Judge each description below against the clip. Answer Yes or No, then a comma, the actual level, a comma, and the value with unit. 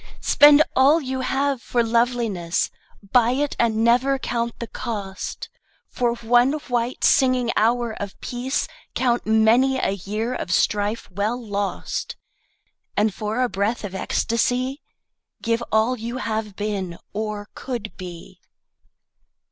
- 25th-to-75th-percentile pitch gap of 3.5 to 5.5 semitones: No, average, 3.1 semitones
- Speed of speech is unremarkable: No, slow, 130 wpm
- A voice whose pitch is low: No, high, 235 Hz